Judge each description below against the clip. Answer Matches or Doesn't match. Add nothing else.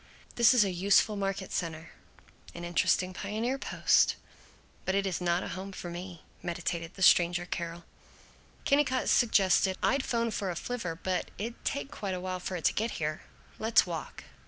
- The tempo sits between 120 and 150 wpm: Doesn't match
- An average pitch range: Matches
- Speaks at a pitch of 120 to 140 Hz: Doesn't match